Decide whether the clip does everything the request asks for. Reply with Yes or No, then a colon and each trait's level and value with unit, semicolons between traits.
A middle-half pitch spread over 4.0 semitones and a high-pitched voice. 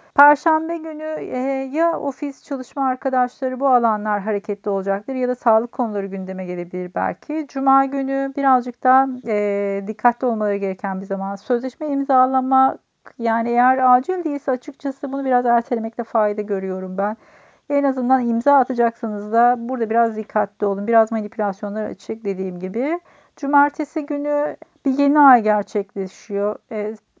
Yes: average, 4.6 semitones; high, 245 Hz